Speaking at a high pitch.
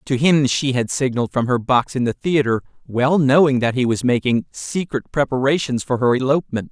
No: low, 130 Hz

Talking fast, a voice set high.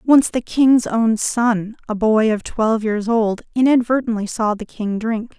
No: average, 180 wpm; high, 225 Hz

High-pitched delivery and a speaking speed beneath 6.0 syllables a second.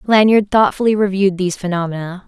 No: high, 195 Hz; 6.5 syllables/s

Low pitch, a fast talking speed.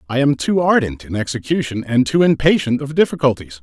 No: low, 130 Hz; average, 180 wpm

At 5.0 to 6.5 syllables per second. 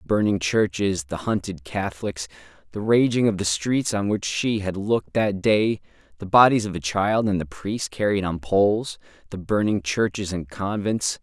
No: 4.8 syllables/s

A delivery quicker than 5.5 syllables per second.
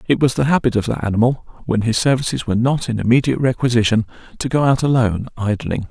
Yes: 6.8 syllables/s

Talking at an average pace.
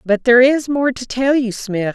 No: fast, 245 wpm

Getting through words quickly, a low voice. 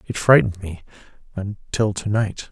No: slow, 120 wpm; low, 100 Hz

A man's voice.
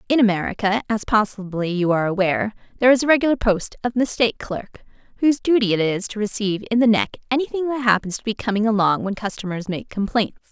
No: female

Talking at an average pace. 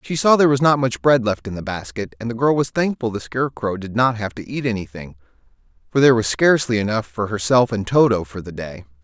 No: fast, 240 wpm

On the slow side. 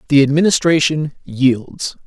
Yes: slow, 85 wpm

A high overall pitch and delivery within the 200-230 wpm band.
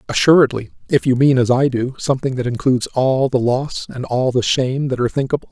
No: low, 130 Hz; fast, 205 wpm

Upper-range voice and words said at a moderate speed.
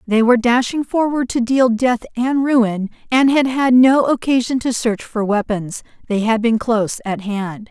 Yes: high, 235 Hz; average, 180 wpm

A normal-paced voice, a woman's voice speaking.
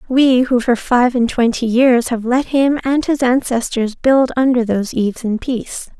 Yes: average, 190 wpm; female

